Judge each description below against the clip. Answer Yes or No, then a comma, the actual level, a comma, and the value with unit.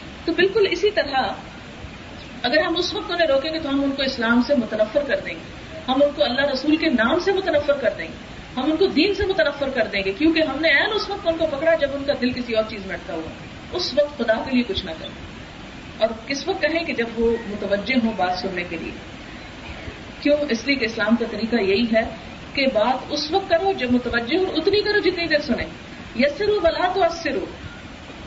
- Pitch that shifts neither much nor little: No, wide, 5.9 semitones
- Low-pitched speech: No, very high, 285 Hz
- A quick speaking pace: Yes, fast, 230 wpm